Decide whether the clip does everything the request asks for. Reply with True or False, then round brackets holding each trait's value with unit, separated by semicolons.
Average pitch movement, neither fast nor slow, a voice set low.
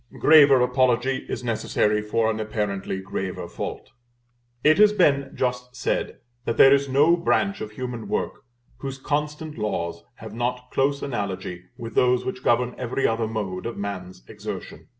True (4.3 semitones; 155 wpm; 125 Hz)